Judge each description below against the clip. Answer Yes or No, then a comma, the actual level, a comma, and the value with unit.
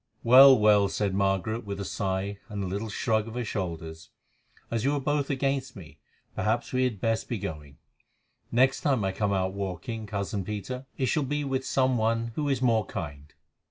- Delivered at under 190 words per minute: No, average, 195 wpm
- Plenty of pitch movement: No, average, 4.8 semitones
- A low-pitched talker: Yes, low, 110 Hz